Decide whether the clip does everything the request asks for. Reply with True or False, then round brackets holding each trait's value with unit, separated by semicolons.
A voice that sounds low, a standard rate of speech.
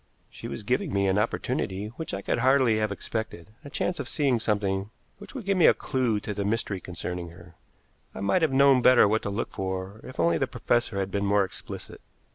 False (105 Hz; 220 wpm)